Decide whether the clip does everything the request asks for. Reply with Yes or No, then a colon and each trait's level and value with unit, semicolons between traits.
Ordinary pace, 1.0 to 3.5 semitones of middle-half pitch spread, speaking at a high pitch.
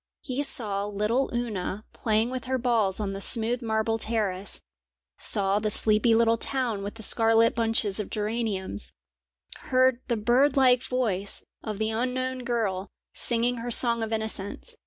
Yes: average, 155 wpm; average, 2.7 semitones; high, 225 Hz